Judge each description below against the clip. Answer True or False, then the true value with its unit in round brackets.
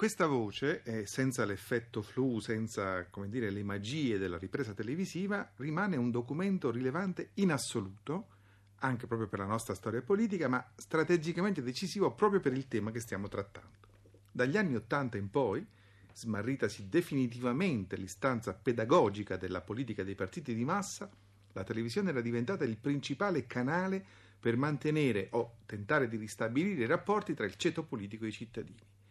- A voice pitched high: False (120 Hz)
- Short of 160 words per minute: True (150 wpm)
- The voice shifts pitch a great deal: True (6.1 semitones)